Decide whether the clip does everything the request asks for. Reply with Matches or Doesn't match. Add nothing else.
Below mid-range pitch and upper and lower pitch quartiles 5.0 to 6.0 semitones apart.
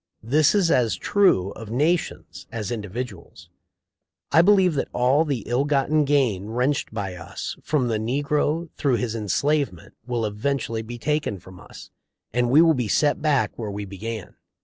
Matches